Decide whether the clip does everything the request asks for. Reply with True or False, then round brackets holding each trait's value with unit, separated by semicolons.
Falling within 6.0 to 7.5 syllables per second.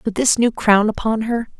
False (5.0 syllables/s)